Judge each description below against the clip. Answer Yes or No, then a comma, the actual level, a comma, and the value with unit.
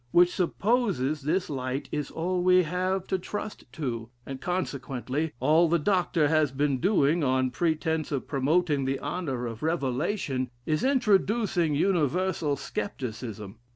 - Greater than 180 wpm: No, slow, 135 wpm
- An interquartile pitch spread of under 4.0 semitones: No, average, 5.2 semitones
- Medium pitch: Yes, medium, 155 Hz